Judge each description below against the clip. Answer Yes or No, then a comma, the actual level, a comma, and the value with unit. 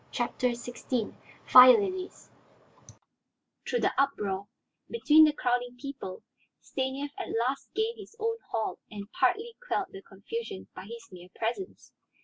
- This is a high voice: Yes, very high, 250 Hz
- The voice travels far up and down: Yes, wide, 8.5 semitones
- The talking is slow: Yes, slow, 130 wpm